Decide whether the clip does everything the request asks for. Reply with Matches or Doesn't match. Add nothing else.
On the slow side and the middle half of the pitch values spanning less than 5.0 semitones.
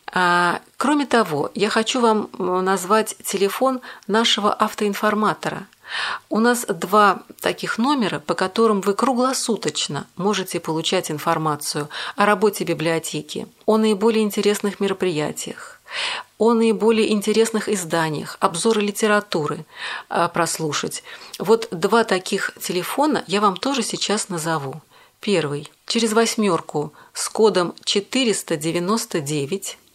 Matches